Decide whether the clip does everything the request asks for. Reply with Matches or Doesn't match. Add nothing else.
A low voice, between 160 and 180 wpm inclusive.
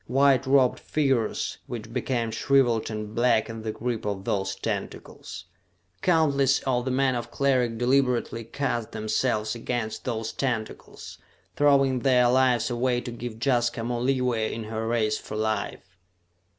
Doesn't match